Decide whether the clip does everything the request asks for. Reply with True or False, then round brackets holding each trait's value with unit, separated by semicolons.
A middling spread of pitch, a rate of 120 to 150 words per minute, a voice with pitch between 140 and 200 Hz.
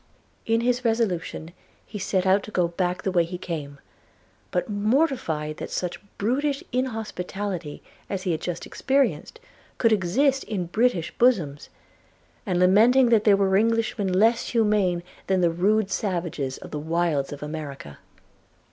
True (4.9 semitones; 145 wpm; 190 Hz)